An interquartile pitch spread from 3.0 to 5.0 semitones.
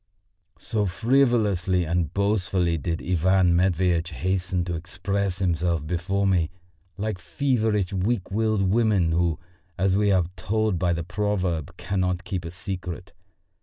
No: narrow, 2.6 semitones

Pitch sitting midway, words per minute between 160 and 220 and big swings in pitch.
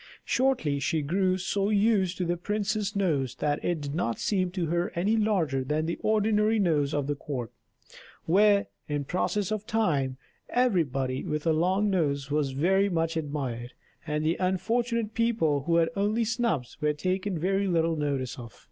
Yes: medium, 175 Hz; average, 165 wpm; wide, 5.7 semitones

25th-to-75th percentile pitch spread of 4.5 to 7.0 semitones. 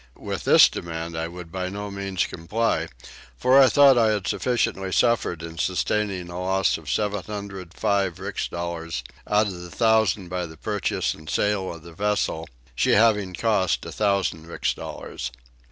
No: average, 3.4 semitones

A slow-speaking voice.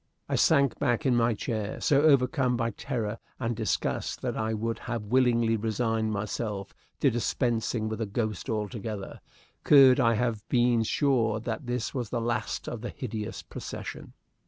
No: average, 165 wpm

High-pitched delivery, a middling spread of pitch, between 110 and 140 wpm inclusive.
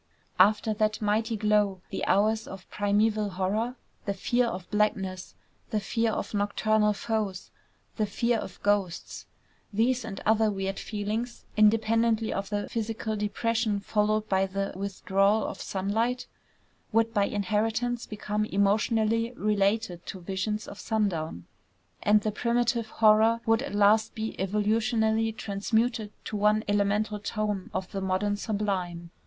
No: high, 210 Hz; narrow, 1.9 semitones; slow, 135 wpm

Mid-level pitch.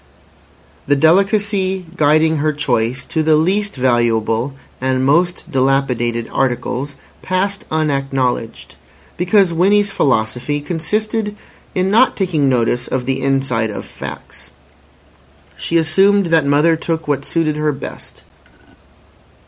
Yes: medium, 150 Hz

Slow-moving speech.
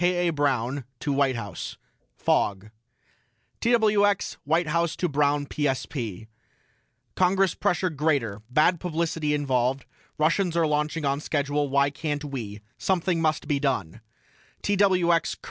Yes: slow, 130 wpm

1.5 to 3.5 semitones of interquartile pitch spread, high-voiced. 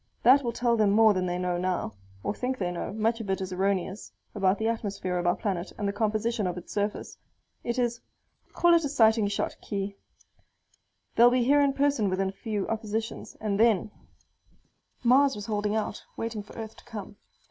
Yes: average, 3.1 semitones; high, 215 Hz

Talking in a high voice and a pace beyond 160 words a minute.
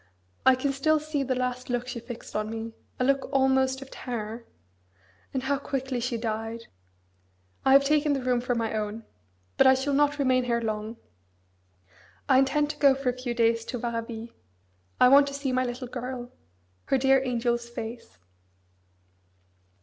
Yes: very high, 255 Hz; average, 170 wpm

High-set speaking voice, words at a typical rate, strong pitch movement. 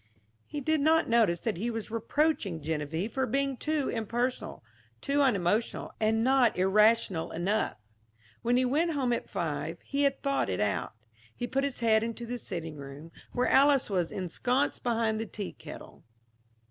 Yes: high, 230 Hz; average, 165 wpm; wide, 6.7 semitones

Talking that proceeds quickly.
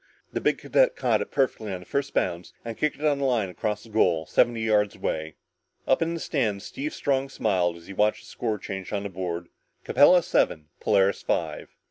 Yes: fast, 210 wpm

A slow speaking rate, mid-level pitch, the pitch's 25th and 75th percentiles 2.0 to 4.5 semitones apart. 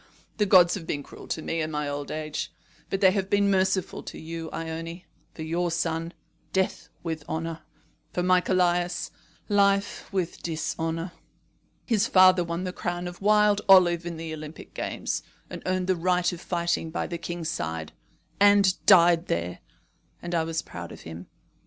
No: average, 170 wpm; medium, 175 Hz; narrow, 2.4 semitones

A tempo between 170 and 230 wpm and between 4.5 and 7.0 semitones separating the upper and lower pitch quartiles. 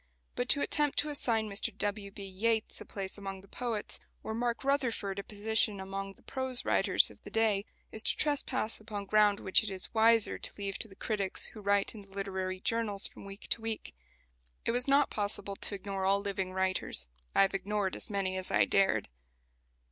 No: average, 200 wpm; narrow, 2.5 semitones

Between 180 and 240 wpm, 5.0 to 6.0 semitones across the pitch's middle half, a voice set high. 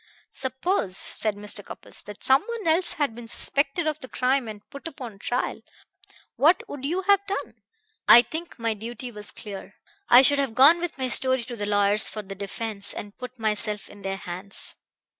Yes: average, 185 wpm; wide, 5.5 semitones; high, 240 Hz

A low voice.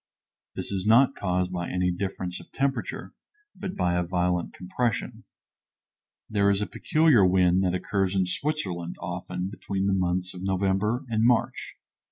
Yes: very low, 95 Hz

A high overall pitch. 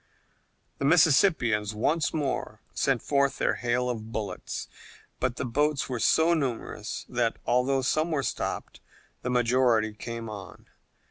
No: low, 125 Hz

